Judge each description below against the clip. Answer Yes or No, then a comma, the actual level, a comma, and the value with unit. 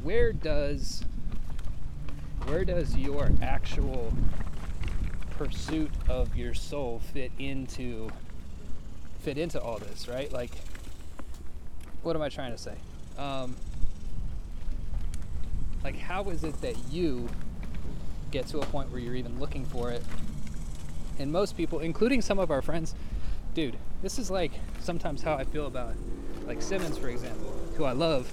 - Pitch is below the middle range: Yes, very low, 90 Hz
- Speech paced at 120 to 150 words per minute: Yes, average, 140 wpm